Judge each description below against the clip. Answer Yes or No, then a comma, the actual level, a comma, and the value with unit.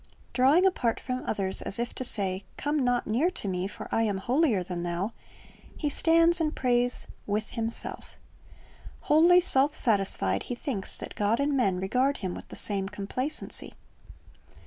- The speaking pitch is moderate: No, high, 240 Hz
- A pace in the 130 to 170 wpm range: Yes, average, 165 wpm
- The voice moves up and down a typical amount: No, wide, 6.4 semitones